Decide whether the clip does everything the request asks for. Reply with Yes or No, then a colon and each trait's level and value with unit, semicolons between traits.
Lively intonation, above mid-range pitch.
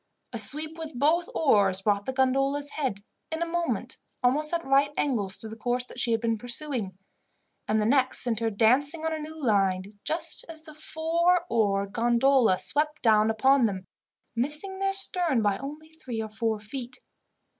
Yes: wide, 5.9 semitones; very high, 260 Hz